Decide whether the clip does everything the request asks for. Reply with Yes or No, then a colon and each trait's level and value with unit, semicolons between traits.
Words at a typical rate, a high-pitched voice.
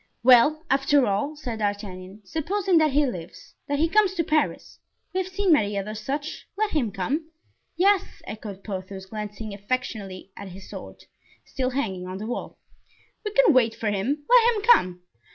Yes: average, 170 wpm; very high, 250 Hz